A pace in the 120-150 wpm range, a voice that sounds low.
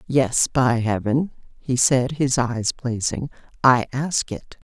Yes: average, 140 wpm; low, 125 Hz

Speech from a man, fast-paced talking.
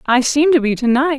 No: female; fast, 305 wpm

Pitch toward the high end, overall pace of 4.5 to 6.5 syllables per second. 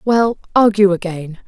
No: high, 200 Hz; 4.3 syllables/s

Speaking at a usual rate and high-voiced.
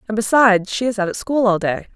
No: fast, 245 wpm; high, 215 Hz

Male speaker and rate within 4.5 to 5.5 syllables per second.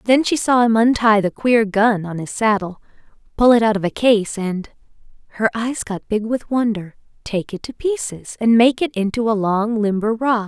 No: female; 4.8 syllables/s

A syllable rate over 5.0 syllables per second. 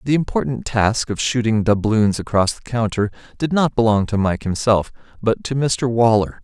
No: 4.9 syllables/s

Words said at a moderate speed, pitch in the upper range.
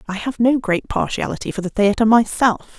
Yes: average, 195 wpm; high, 220 Hz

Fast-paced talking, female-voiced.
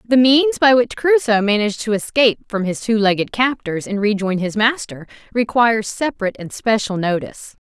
No: average, 170 wpm; female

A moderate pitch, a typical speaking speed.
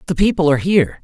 No: medium, 160 Hz; fast, 235 wpm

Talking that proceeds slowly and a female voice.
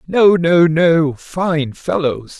No: slow, 125 wpm; male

